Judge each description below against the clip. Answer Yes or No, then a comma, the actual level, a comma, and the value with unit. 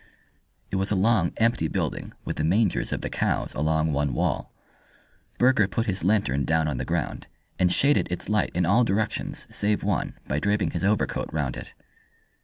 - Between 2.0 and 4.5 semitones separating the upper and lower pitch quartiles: No, average, 5.1 semitones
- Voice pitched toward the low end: Yes, very low, 95 Hz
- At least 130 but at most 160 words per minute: No, average, 185 wpm